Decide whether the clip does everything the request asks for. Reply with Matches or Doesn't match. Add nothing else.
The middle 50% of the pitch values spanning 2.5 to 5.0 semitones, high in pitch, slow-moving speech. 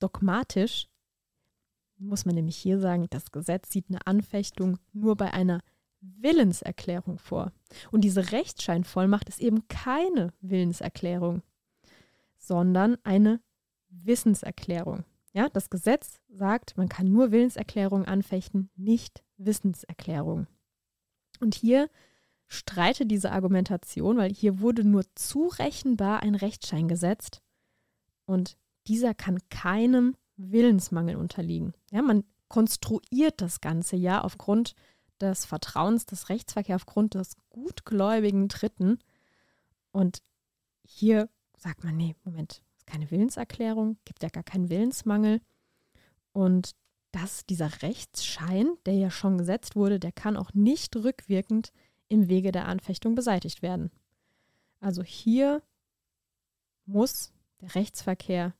Matches